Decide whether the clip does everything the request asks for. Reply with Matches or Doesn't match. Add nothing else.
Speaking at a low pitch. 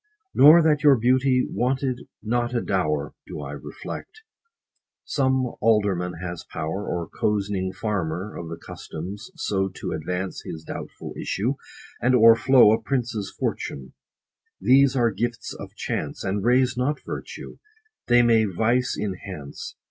Matches